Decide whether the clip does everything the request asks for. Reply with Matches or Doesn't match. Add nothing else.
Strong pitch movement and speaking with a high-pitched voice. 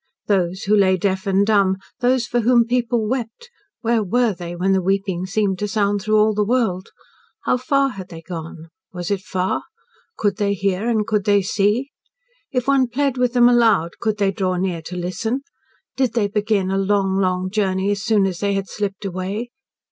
Doesn't match